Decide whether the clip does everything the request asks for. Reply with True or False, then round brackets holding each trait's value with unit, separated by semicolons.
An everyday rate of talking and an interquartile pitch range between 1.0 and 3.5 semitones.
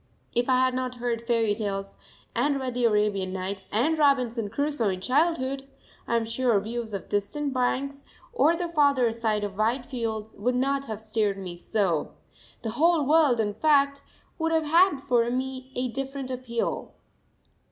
False (170 wpm; 4.2 semitones)